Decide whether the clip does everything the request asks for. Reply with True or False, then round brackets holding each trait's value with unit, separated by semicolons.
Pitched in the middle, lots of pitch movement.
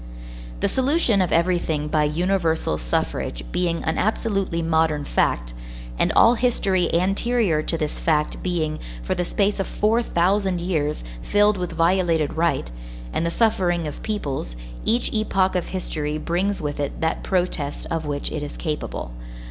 False (170 Hz; 4.2 semitones)